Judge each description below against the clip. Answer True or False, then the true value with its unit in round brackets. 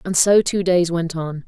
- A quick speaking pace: True (245 wpm)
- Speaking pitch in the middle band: True (175 Hz)